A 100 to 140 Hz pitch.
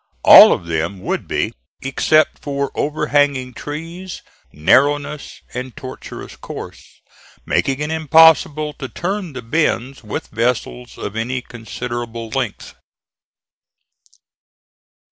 Yes: low, 135 Hz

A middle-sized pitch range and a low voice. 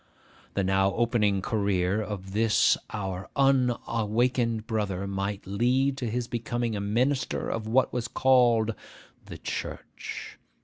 Yes: average, 3.3 semitones; low, 110 Hz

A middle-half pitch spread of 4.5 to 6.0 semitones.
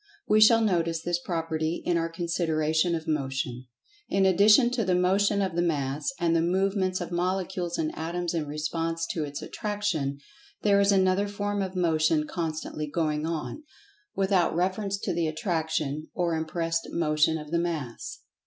No: average, 3.2 semitones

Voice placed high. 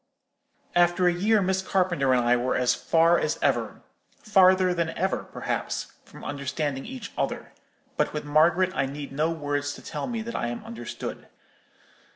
No: medium, 165 Hz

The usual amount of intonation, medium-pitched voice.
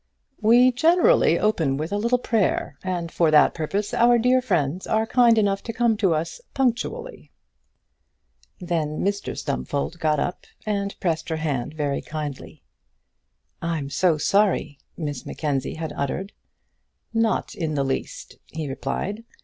No: wide, 6.5 semitones; medium, 175 Hz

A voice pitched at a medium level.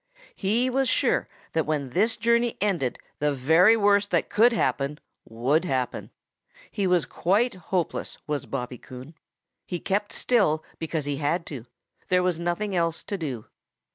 Yes: medium, 170 Hz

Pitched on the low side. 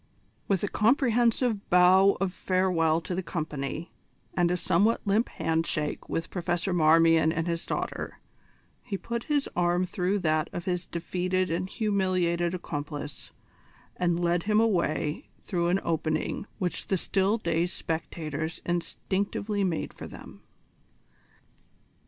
No: medium, 175 Hz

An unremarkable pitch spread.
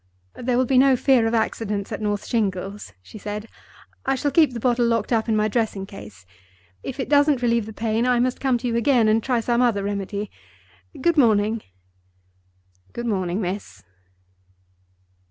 Yes: average, 3.3 semitones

